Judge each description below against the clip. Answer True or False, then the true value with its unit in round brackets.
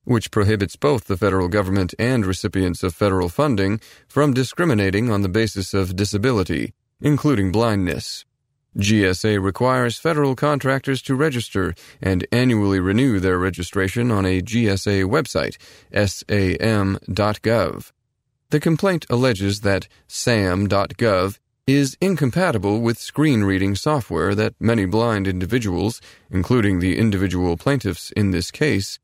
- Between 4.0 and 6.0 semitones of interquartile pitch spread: True (4.7 semitones)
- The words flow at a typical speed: False (120 wpm)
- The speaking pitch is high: False (105 Hz)